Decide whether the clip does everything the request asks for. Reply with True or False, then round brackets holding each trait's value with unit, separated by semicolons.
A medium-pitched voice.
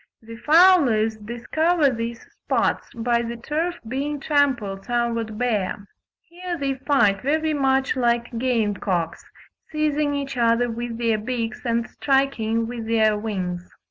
False (240 Hz)